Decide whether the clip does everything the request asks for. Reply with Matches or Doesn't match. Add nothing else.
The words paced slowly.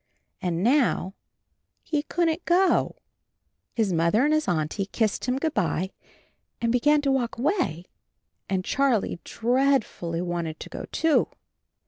Matches